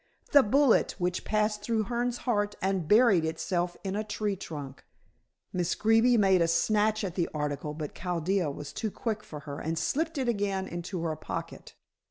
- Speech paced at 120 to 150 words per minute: No, average, 180 wpm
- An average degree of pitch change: Yes, average, 4.6 semitones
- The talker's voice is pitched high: Yes, high, 195 Hz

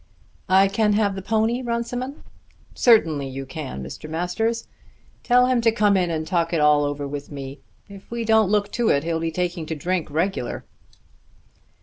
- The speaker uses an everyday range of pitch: No, wide, 6.3 semitones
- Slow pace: No, average, 180 wpm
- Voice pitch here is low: No, medium, 185 Hz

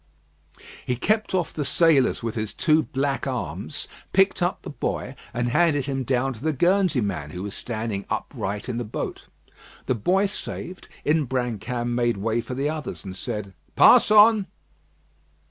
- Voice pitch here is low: Yes, low, 130 Hz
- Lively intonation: Yes, wide, 6.1 semitones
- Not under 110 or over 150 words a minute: No, average, 165 wpm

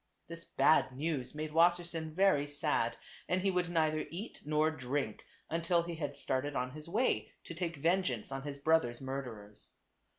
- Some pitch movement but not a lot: Yes, average, 3.8 semitones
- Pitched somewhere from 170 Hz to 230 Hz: No, medium, 155 Hz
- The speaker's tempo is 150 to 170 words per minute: Yes, average, 165 wpm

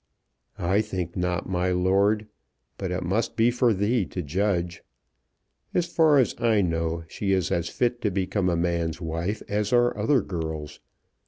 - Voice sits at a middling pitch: No, very low, 95 Hz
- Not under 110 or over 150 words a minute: No, average, 165 wpm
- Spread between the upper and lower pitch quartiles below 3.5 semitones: No, average, 3.9 semitones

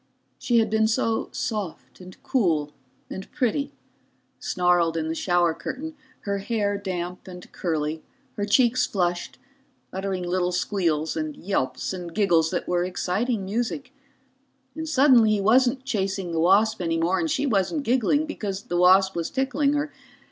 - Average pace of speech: Yes, average, 155 wpm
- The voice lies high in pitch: Yes, high, 195 Hz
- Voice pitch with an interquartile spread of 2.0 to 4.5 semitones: No, average, 5.0 semitones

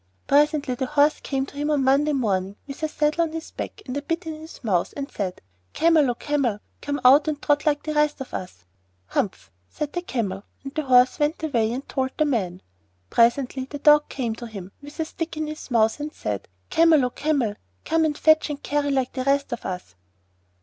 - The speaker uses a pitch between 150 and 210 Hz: No, very high, 280 Hz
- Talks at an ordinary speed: No, fast, 220 wpm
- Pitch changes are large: No, average, 3.8 semitones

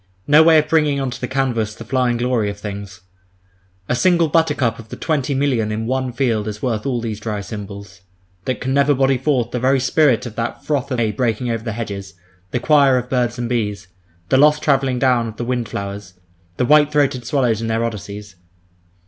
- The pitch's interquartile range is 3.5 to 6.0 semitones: Yes, average, 3.9 semitones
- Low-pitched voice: Yes, low, 120 Hz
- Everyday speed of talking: No, fast, 210 wpm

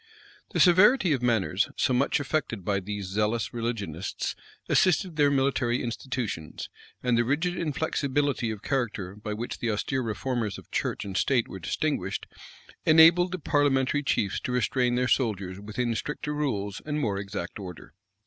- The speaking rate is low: No, average, 155 wpm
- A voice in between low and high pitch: No, low, 120 Hz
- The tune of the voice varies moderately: No, wide, 5.8 semitones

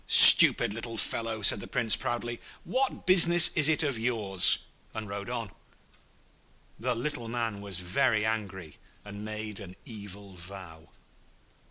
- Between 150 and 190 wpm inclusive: No, average, 140 wpm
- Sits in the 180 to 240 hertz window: No, low, 110 Hz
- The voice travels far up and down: No, average, 3.2 semitones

